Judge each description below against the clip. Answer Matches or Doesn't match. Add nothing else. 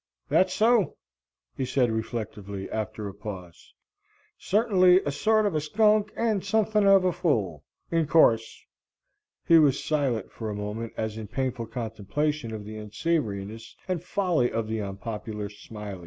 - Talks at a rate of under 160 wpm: Matches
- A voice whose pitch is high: Doesn't match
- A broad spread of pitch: Matches